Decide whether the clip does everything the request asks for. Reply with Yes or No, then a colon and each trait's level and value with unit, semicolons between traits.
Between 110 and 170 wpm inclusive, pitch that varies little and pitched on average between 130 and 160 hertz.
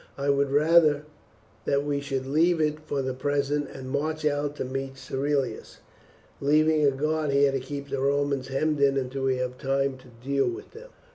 No: average, 190 wpm; narrow, 1.8 semitones; medium, 140 Hz